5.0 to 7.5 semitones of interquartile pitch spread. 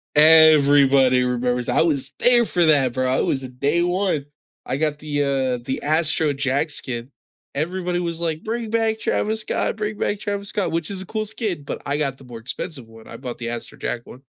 Yes: wide, 5.4 semitones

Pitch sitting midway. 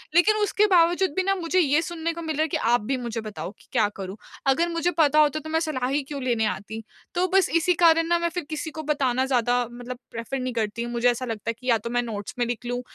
No: very high, 270 Hz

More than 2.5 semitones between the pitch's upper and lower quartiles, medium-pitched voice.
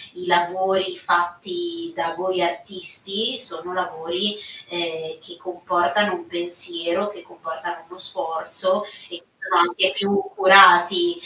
No: narrow, 1.9 semitones; medium, 180 Hz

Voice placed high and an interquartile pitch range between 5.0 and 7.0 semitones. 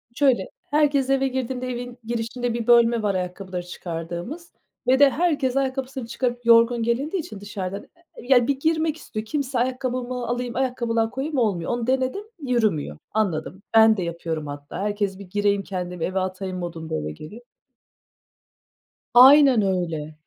Yes: high, 235 Hz; wide, 5.6 semitones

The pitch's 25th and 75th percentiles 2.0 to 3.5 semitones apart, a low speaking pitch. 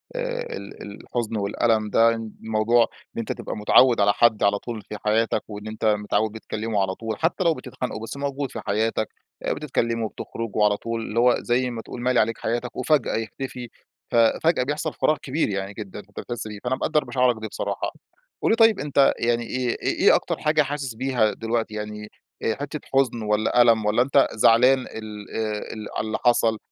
Yes: average, 3.0 semitones; low, 115 Hz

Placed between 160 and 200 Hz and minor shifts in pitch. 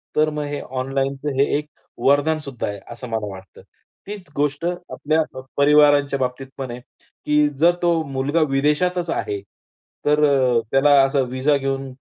No: medium, 140 Hz; narrow, 2.1 semitones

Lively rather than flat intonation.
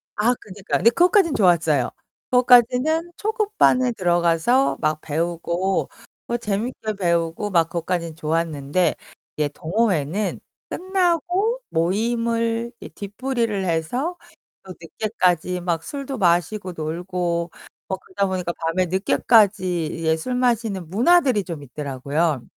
Yes: wide, 6.2 semitones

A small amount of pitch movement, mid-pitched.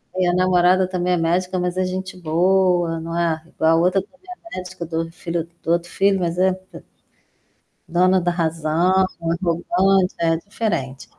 Yes: narrow, 2.0 semitones; medium, 180 Hz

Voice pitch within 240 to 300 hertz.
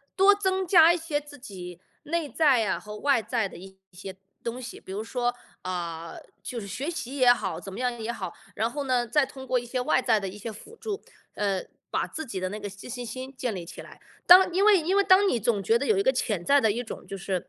Yes: high, 245 Hz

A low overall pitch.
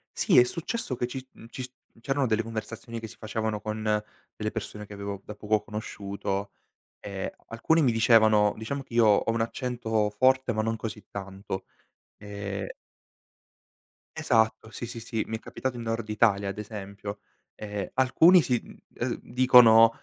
Yes: low, 110 Hz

